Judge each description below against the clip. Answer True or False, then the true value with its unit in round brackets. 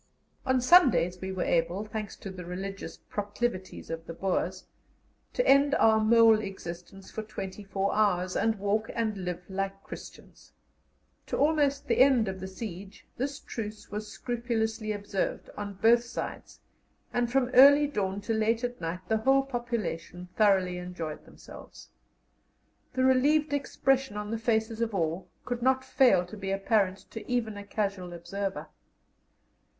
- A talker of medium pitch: False (215 Hz)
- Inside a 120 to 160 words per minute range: True (155 wpm)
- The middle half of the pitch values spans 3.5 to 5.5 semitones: True (4.0 semitones)